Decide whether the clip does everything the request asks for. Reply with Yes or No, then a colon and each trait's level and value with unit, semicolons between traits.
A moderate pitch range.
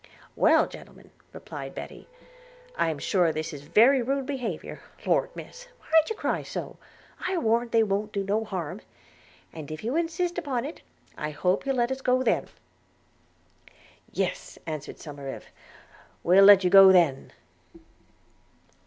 No: wide, 7.9 semitones